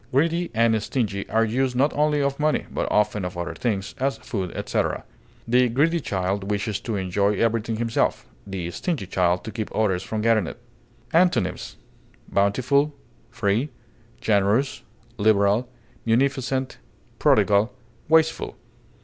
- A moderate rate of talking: No, slow, 130 wpm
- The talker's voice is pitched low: Yes, low, 110 Hz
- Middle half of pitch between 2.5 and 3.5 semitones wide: No, average, 5.0 semitones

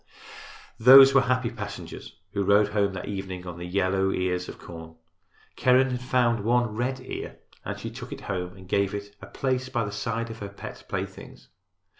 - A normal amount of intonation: Yes, average, 4.5 semitones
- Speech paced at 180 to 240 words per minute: Yes, average, 190 wpm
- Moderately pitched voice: No, low, 105 Hz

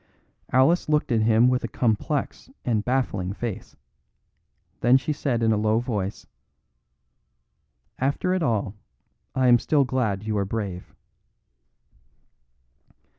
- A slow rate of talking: Yes, slow, 125 wpm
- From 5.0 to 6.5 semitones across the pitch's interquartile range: No, average, 3.6 semitones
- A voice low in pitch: Yes, low, 120 Hz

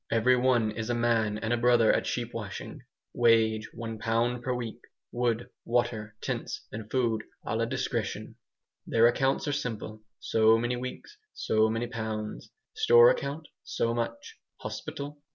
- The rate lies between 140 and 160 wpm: Yes, average, 150 wpm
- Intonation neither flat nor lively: No, narrow, 1.9 semitones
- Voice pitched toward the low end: Yes, low, 115 Hz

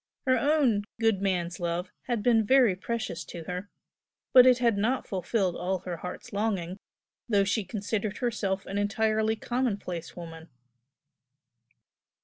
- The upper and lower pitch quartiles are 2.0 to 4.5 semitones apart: Yes, average, 4.1 semitones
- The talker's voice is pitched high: Yes, high, 205 Hz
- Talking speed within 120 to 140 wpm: Yes, slow, 135 wpm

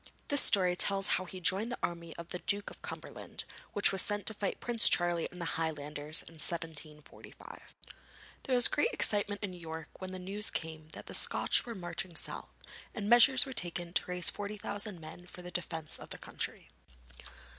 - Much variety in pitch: No, average, 3.7 semitones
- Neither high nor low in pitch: Yes, medium, 180 Hz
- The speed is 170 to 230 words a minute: Yes, average, 190 wpm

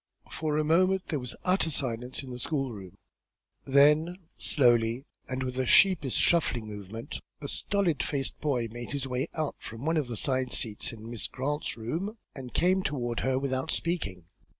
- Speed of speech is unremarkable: Yes, average, 180 wpm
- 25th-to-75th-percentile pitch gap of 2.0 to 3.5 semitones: No, average, 4.5 semitones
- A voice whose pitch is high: No, low, 130 Hz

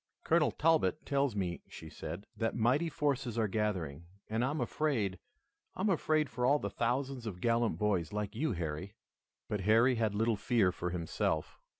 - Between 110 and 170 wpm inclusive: No, average, 180 wpm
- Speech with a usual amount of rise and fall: No, wide, 6.0 semitones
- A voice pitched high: No, low, 115 Hz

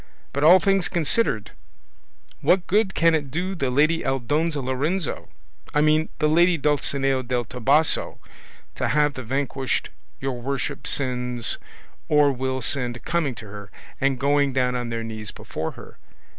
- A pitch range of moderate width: Yes, average, 3.7 semitones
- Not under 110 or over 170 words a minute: Yes, average, 150 wpm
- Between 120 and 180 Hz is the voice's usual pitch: Yes, medium, 140 Hz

